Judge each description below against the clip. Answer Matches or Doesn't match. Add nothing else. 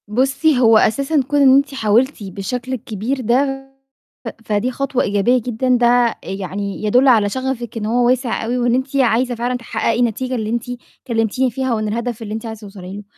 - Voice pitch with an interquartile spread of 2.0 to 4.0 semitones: Matches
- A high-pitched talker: Matches